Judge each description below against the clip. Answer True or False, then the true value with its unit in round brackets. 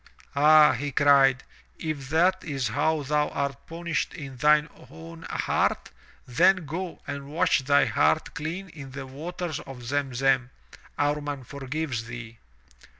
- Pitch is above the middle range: False (145 Hz)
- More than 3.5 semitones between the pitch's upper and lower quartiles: False (2.9 semitones)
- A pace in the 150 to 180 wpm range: False (140 wpm)